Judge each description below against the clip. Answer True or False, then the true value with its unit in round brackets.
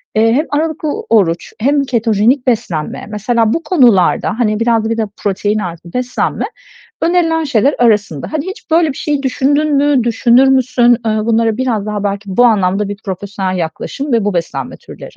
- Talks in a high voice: True (230 Hz)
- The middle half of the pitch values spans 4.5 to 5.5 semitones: True (4.9 semitones)